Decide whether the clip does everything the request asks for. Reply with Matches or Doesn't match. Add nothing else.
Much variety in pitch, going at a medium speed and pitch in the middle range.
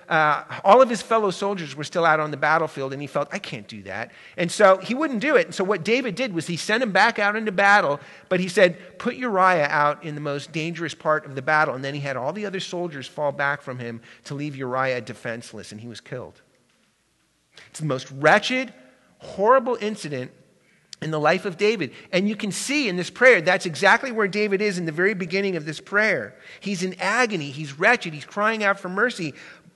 Doesn't match